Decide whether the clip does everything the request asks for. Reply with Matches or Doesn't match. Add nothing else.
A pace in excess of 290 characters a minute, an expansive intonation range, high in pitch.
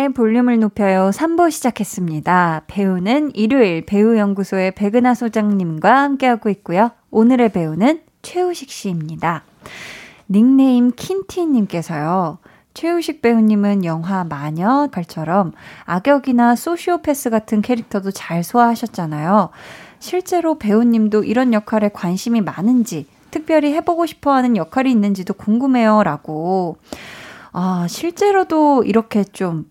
Matches